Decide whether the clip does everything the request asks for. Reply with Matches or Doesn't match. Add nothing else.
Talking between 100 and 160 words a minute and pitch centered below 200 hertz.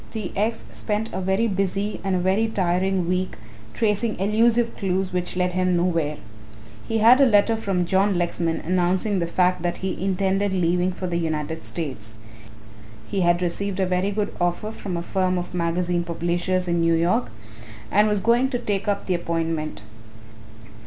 Doesn't match